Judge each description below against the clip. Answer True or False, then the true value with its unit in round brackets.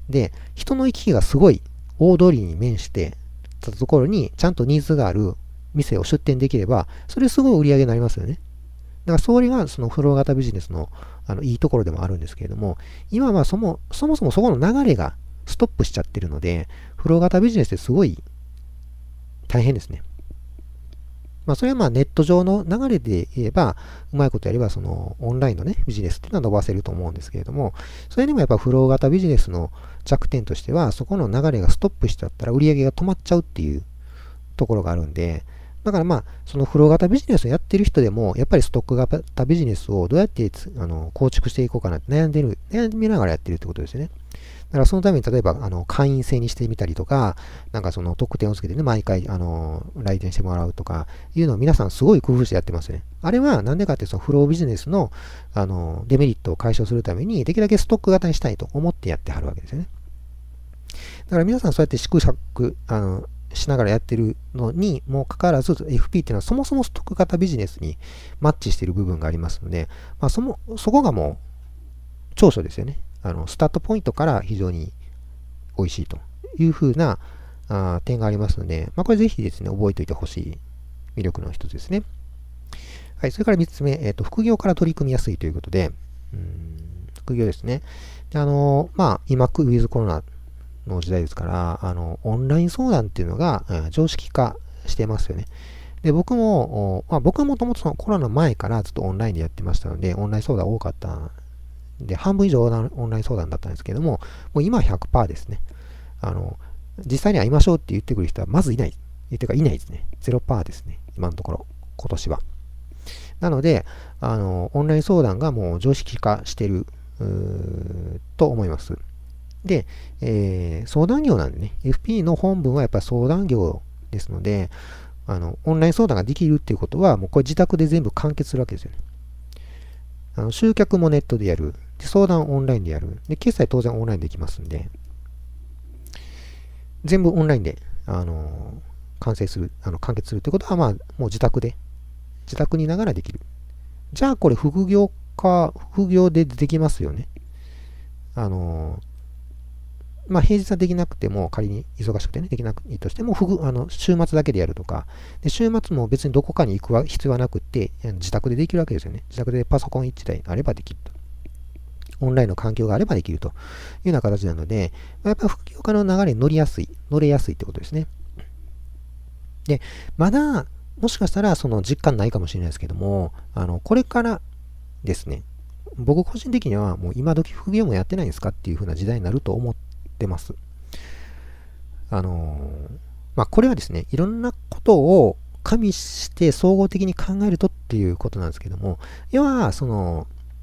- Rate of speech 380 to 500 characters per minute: True (395 characters per minute)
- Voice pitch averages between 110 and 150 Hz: False (100 Hz)